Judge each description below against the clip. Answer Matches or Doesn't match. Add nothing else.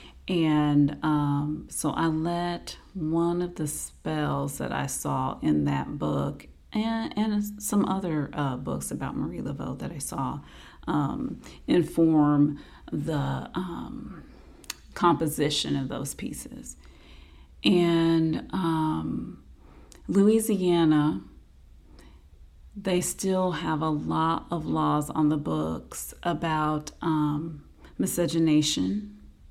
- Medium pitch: Matches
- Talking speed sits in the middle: Doesn't match